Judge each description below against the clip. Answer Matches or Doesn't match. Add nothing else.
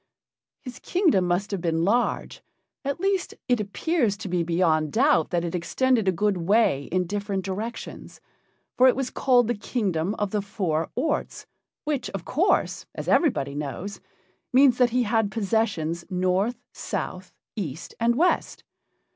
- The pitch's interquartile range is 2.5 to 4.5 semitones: Doesn't match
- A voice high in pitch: Matches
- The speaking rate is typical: Matches